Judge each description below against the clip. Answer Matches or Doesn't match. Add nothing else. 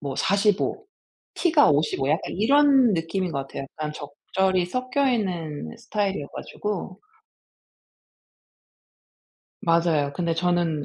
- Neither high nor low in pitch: Matches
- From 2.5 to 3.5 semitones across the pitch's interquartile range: Doesn't match